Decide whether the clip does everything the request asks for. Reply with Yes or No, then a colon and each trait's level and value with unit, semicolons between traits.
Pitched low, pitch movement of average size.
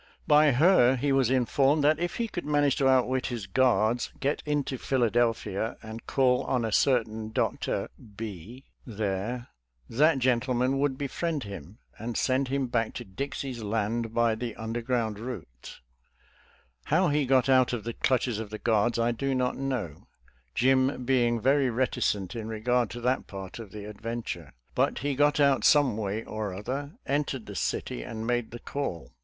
Yes: low, 120 Hz; average, 3.5 semitones